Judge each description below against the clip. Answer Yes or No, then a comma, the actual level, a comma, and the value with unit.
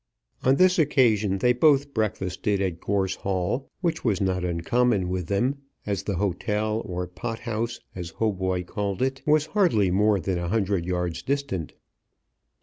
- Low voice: Yes, low, 100 Hz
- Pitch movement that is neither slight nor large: Yes, average, 5.0 semitones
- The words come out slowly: No, average, 155 wpm